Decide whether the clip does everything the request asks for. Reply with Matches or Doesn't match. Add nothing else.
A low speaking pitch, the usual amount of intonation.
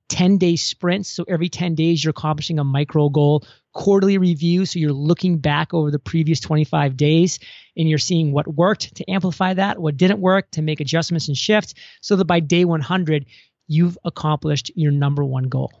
Doesn't match